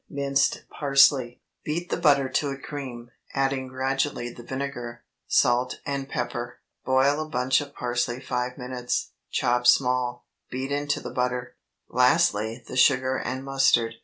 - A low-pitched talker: Yes, low, 130 Hz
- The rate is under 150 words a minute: Yes, average, 140 wpm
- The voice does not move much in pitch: Yes, narrow, 2.1 semitones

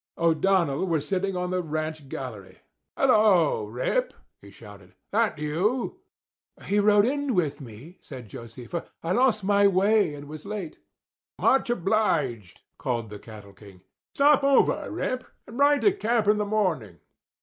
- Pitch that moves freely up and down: Yes, wide, 7.8 semitones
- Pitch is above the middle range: No, medium, 180 Hz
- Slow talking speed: No, average, 145 wpm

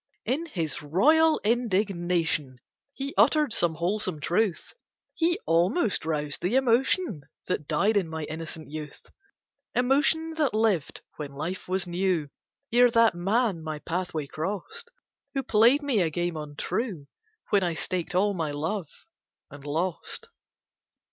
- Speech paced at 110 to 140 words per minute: Yes, slow, 135 wpm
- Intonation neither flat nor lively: No, wide, 6.7 semitones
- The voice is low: No, medium, 185 Hz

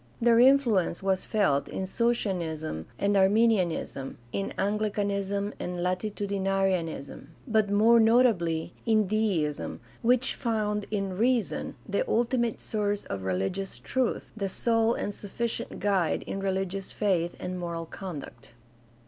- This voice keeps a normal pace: No, slow, 125 wpm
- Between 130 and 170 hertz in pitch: No, high, 200 Hz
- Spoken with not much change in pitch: No, average, 3.5 semitones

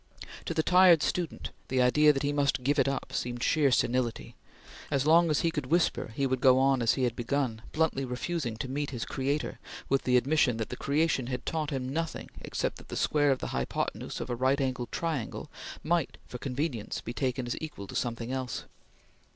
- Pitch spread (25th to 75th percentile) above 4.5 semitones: No, average, 3.2 semitones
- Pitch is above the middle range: No, low, 135 Hz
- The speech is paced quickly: Yes, fast, 210 wpm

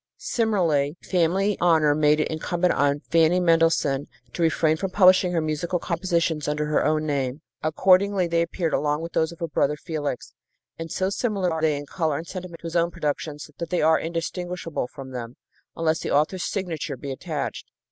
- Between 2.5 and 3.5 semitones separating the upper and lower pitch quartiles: Yes, average, 2.9 semitones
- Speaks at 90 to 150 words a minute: No, average, 185 wpm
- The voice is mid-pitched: Yes, medium, 165 Hz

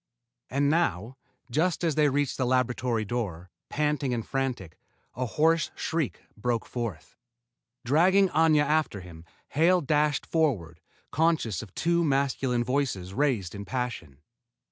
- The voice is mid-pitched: No, low, 130 Hz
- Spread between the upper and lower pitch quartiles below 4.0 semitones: No, wide, 5.5 semitones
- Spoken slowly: Yes, slow, 130 wpm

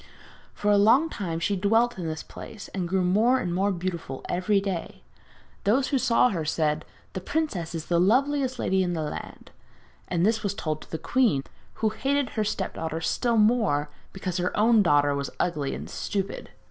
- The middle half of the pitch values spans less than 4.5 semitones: No, average, 5.1 semitones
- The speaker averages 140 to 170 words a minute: No, average, 185 wpm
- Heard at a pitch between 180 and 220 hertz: Yes, high, 190 Hz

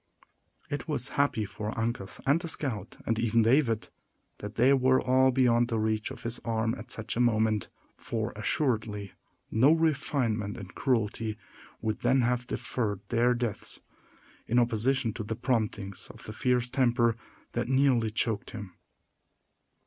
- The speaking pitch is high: No, low, 115 Hz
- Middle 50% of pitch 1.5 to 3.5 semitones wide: Yes, average, 2.9 semitones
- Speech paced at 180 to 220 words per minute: No, average, 150 wpm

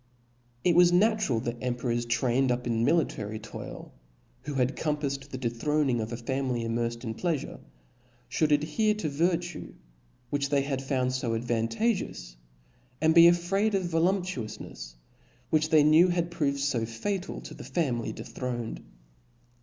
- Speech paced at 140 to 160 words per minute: Yes, average, 145 wpm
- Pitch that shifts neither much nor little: No, wide, 6.2 semitones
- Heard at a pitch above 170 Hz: No, medium, 140 Hz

